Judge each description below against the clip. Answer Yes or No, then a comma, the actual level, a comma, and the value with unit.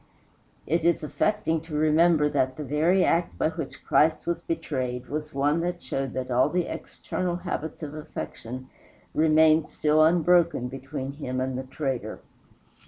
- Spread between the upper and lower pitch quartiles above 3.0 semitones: Yes, average, 3.7 semitones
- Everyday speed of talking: Yes, average, 155 wpm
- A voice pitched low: No, medium, 155 Hz